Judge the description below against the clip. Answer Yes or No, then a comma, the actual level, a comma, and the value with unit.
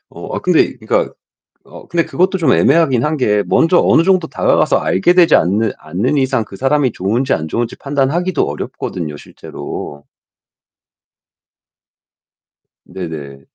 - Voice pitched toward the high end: No, low, 130 Hz